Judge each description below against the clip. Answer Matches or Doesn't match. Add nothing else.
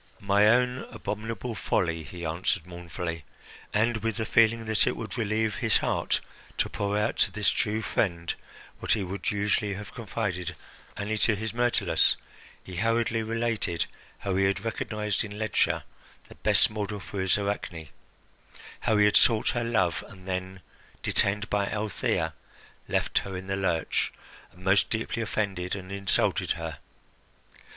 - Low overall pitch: Matches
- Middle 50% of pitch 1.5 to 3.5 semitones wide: Matches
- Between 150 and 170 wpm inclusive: Matches